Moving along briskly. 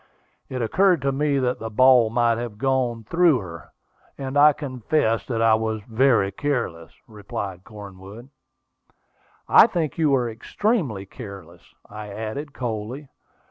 No: average, 140 wpm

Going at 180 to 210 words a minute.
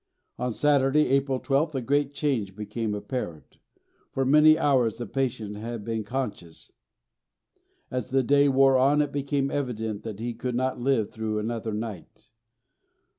No: average, 150 wpm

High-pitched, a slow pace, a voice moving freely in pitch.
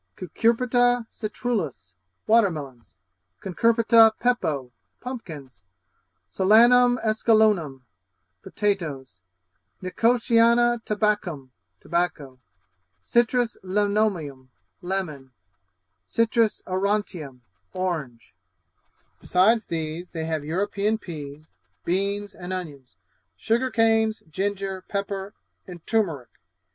Yes: high, 195 Hz; slow, 75 wpm; wide, 6.1 semitones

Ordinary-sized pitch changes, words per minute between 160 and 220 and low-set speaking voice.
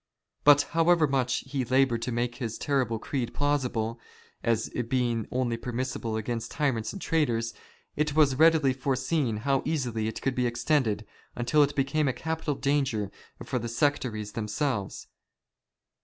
No: average, 3.8 semitones; average, 145 wpm; low, 130 Hz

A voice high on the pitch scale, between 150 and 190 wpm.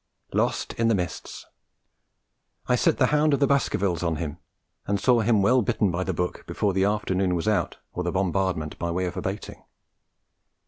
No: very low, 95 Hz; average, 185 wpm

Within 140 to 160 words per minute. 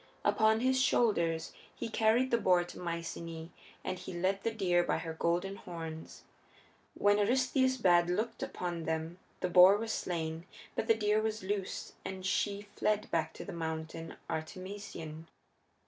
Yes: average, 155 wpm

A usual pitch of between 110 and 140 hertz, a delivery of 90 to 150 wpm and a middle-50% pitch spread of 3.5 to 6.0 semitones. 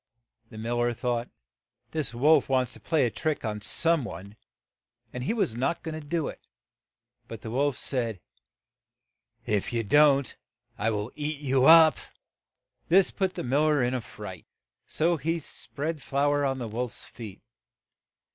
No: low, 135 Hz; average, 175 wpm; average, 4.7 semitones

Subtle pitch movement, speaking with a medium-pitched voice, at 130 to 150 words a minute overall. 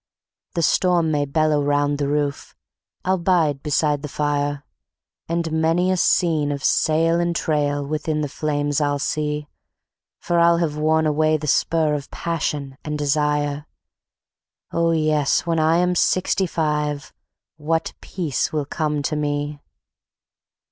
Yes: narrow, 2.1 semitones; medium, 150 Hz; average, 140 wpm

